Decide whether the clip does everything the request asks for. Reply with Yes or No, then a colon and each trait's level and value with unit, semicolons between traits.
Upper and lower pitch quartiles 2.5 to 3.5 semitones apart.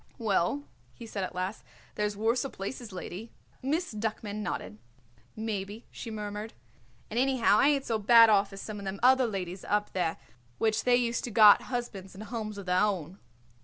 Yes: average, 3.0 semitones